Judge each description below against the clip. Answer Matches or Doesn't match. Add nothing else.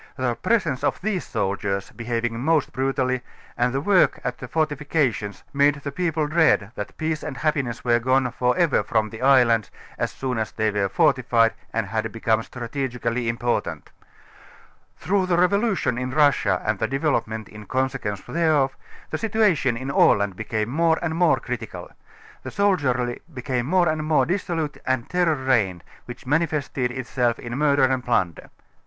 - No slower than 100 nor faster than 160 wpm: Doesn't match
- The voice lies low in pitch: Matches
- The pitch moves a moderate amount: Matches